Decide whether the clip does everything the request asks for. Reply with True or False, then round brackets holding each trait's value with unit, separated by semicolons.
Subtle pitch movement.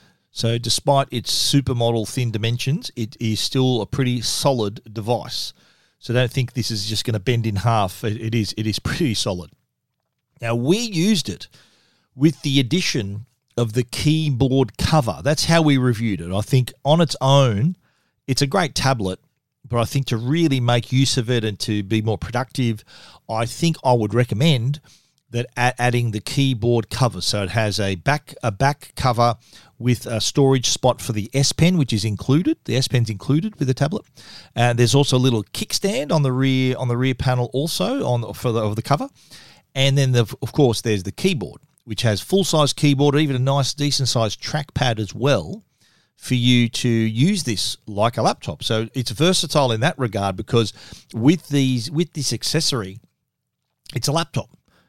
False (3.7 semitones)